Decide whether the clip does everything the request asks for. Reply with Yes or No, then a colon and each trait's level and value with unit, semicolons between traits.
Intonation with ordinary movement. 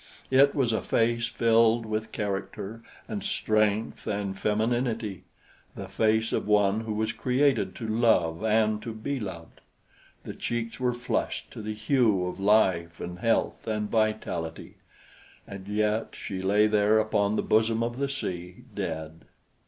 No: narrow, 2.3 semitones